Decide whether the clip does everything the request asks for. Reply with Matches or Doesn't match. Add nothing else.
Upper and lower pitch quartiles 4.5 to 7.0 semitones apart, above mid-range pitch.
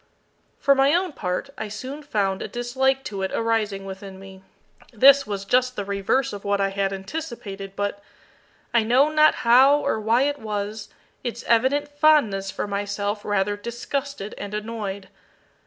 Matches